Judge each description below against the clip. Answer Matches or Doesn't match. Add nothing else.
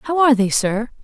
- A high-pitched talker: Matches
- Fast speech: Matches